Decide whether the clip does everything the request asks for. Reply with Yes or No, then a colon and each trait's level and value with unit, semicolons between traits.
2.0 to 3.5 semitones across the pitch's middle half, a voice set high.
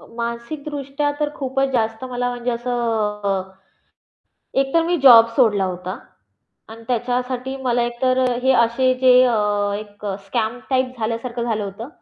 Yes: narrow, 2.6 semitones; high, 240 Hz